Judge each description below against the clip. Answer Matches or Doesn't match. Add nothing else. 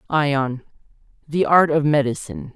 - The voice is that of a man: Matches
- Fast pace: Doesn't match